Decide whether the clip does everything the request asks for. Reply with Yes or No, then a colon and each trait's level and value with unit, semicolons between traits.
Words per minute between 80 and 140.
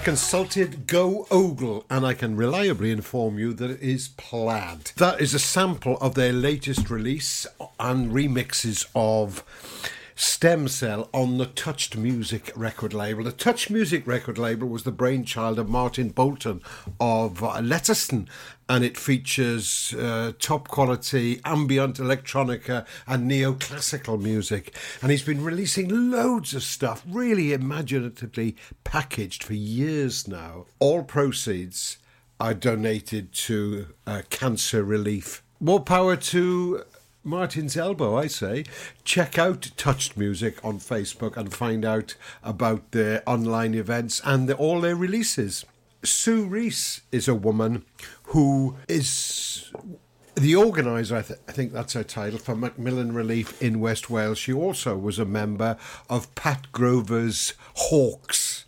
Yes: slow, 135 wpm